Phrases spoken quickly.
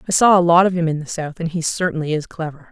Yes: fast, 310 wpm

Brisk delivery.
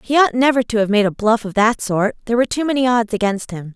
Yes: fast, 290 wpm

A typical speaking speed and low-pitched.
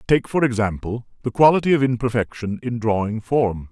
Yes: average, 160 wpm; low, 120 Hz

